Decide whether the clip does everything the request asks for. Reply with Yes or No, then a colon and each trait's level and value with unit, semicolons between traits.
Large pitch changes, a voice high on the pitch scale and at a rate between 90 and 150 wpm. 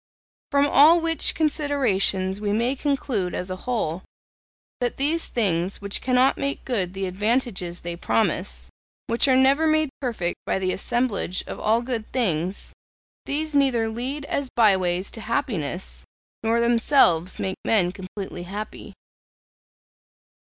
Yes: wide, 6.2 semitones; high, 225 Hz; average, 140 wpm